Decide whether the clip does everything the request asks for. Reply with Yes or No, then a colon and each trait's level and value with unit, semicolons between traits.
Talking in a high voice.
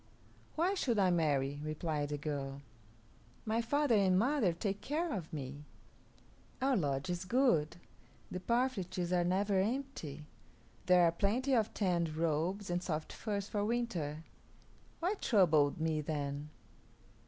No: medium, 180 Hz